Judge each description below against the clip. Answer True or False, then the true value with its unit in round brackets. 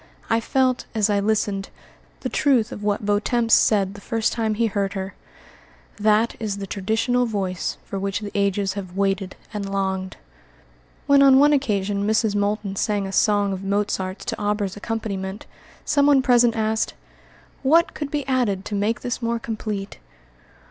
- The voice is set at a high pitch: True (210 Hz)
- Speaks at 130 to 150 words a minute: False (160 wpm)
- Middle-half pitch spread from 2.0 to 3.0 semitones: True (2.7 semitones)